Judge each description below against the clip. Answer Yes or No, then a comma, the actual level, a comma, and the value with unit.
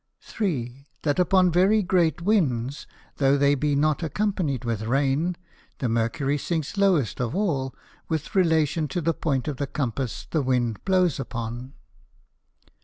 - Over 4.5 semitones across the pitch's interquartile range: Yes, average, 5.0 semitones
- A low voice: No, medium, 145 Hz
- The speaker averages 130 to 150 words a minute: Yes, average, 145 wpm